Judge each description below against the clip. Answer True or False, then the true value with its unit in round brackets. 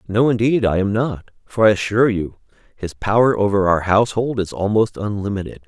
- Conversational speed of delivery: True (180 wpm)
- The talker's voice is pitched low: True (105 Hz)